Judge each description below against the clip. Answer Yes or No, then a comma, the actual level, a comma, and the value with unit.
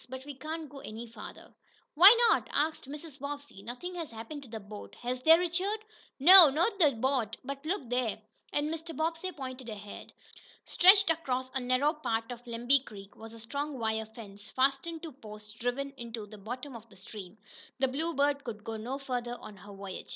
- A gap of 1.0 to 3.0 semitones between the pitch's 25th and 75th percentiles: No, average, 5.0 semitones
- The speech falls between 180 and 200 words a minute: Yes, average, 195 wpm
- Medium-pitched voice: No, very high, 260 Hz